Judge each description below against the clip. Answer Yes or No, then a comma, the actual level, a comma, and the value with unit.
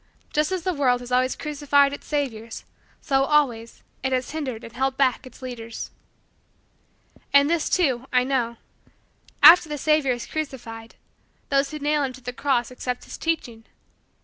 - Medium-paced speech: Yes, average, 165 wpm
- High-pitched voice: Yes, very high, 265 Hz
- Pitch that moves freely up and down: No, average, 3.1 semitones